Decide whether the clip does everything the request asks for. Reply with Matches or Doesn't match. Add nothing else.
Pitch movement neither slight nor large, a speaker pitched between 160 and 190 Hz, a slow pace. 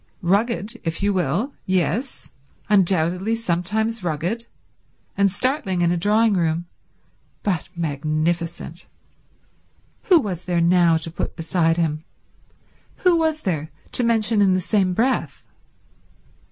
Matches